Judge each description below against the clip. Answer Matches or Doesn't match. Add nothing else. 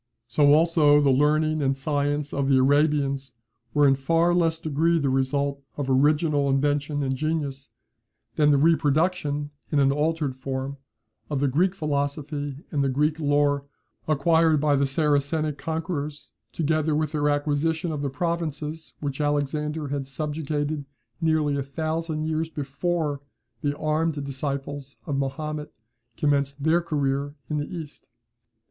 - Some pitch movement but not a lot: Doesn't match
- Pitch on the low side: Doesn't match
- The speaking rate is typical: Matches